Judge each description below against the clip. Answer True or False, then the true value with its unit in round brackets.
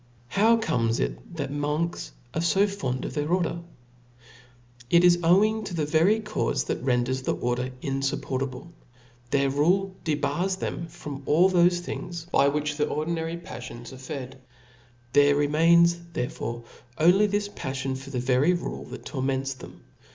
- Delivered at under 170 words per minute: True (160 wpm)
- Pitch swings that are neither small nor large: True (4.7 semitones)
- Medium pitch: True (150 Hz)